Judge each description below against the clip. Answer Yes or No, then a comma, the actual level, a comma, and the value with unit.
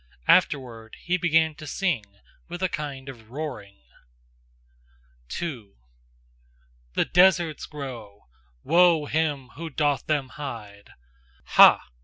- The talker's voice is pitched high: No, medium, 145 Hz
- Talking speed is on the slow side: Yes, slow, 105 wpm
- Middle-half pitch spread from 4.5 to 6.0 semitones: Yes, average, 4.9 semitones